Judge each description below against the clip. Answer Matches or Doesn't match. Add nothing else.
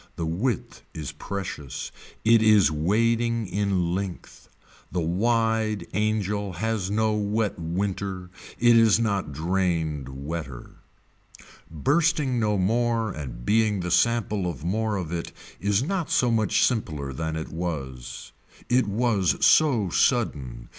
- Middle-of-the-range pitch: Doesn't match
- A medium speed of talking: Doesn't match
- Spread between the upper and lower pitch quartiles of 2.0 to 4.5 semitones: Doesn't match